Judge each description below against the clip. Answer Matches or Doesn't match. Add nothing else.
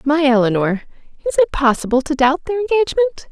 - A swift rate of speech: Doesn't match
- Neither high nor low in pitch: Doesn't match